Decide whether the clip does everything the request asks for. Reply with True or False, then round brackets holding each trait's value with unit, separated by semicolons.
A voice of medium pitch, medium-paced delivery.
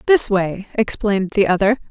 False (205 Hz; 160 wpm)